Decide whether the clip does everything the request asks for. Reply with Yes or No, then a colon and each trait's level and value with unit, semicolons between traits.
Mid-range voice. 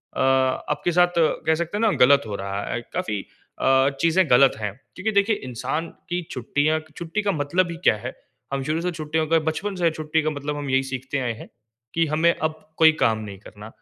Yes: medium, 155 Hz